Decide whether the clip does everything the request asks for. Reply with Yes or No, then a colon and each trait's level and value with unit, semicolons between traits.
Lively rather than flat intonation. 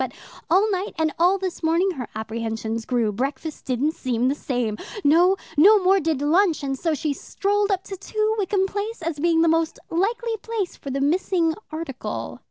Yes: wide, 6.1 semitones